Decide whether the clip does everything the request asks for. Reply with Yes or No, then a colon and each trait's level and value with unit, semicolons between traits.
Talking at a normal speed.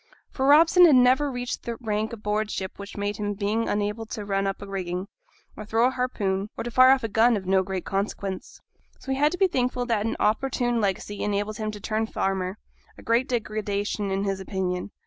No: fast, 220 wpm